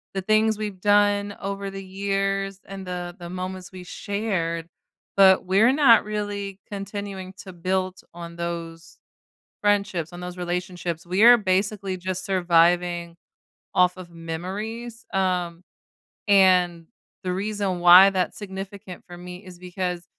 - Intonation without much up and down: Yes, narrow, 2.2 semitones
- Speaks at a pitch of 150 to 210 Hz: Yes, medium, 185 Hz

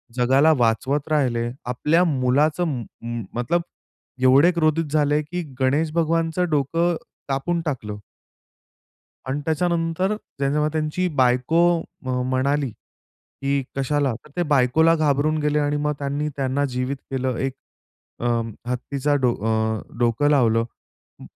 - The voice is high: No, medium, 145 Hz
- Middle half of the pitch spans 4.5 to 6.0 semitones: No, average, 3.3 semitones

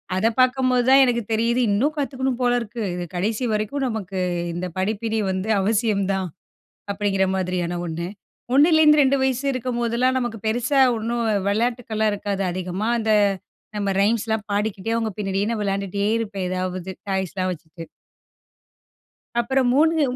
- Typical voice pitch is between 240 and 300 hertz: No, high, 220 Hz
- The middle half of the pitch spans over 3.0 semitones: Yes, average, 4.1 semitones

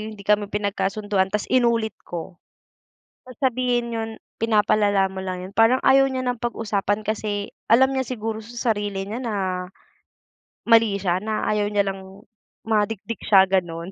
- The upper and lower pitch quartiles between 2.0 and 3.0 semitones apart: Yes, narrow, 2.6 semitones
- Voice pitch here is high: Yes, high, 210 Hz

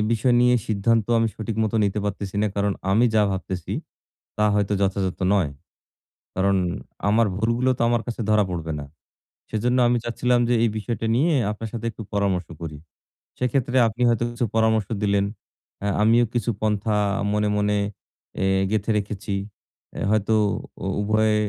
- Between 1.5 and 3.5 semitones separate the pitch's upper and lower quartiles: Yes, narrow, 2.6 semitones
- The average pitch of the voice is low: Yes, low, 105 Hz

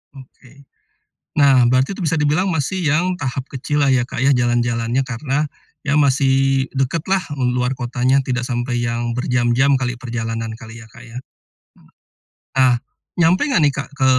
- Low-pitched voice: Yes, low, 130 Hz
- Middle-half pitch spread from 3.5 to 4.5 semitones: No, average, 3.0 semitones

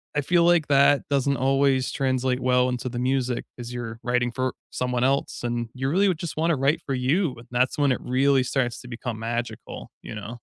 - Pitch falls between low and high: No, low, 130 Hz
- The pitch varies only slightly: Yes, narrow, 2.3 semitones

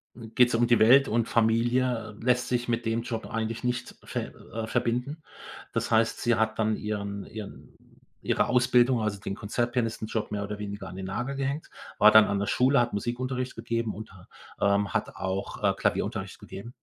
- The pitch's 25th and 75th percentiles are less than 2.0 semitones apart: No, narrow, 2.6 semitones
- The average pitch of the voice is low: Yes, low, 115 Hz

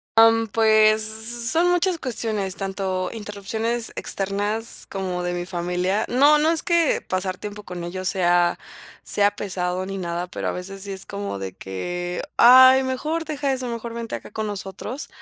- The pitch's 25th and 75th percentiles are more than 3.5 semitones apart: Yes, average, 4.1 semitones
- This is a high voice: Yes, high, 205 Hz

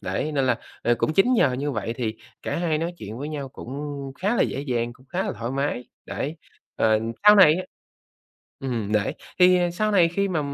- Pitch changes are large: Yes, wide, 6.0 semitones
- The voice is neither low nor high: Yes, medium, 145 Hz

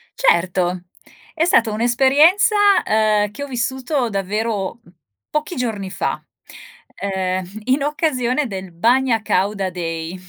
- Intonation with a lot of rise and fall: Yes, wide, 5.8 semitones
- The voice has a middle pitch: No, high, 220 Hz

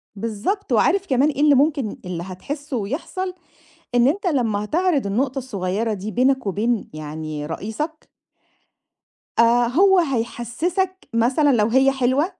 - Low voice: No, very high, 255 Hz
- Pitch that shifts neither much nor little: No, wide, 6.0 semitones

